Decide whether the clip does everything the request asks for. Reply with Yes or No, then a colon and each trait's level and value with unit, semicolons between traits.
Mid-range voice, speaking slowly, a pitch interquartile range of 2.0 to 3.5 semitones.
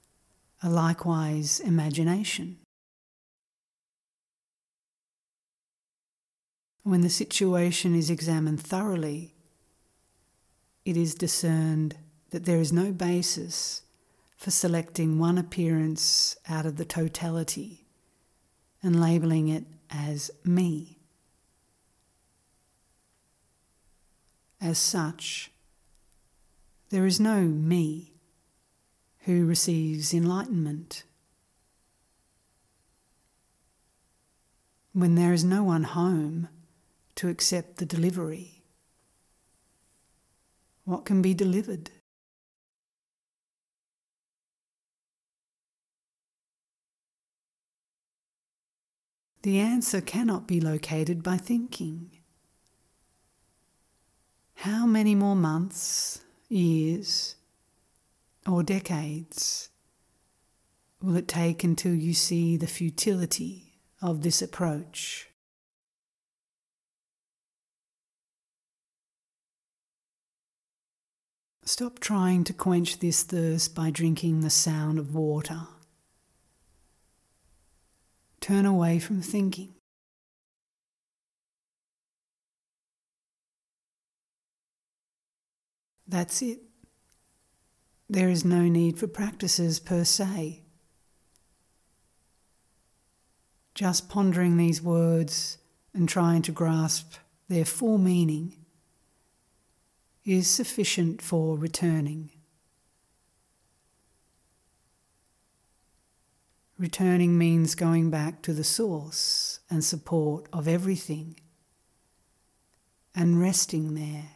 Yes: medium, 165 Hz; slow, 70 wpm; narrow, 2.4 semitones